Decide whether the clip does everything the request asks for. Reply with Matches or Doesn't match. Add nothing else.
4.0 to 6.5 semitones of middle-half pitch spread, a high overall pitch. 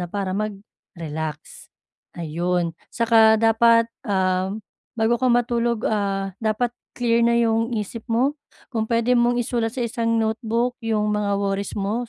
Doesn't match